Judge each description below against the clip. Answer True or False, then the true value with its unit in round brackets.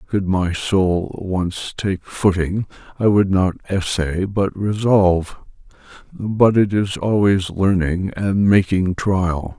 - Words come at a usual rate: False (125 wpm)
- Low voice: True (95 Hz)